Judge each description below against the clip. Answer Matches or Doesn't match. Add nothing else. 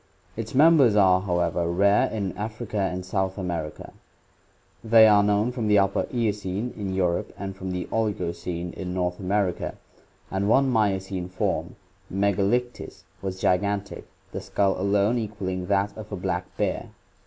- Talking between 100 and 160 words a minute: Matches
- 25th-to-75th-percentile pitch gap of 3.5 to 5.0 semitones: Doesn't match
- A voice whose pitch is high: Doesn't match